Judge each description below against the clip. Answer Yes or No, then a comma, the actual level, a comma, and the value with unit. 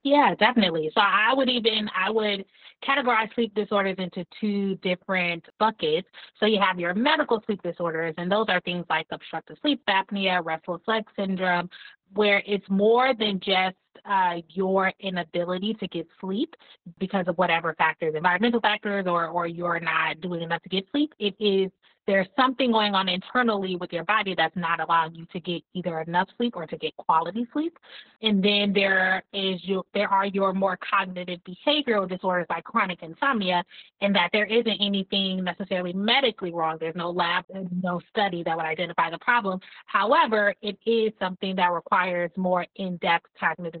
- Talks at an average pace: Yes, average, 175 wpm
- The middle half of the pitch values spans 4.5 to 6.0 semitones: No, average, 3.3 semitones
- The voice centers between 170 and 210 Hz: Yes, high, 190 Hz